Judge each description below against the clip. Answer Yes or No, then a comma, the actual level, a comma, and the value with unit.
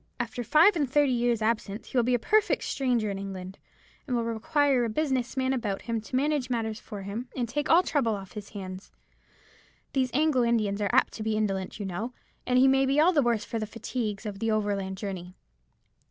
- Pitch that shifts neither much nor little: Yes, average, 4.1 semitones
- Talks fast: Yes, fast, 215 wpm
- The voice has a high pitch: Yes, high, 230 Hz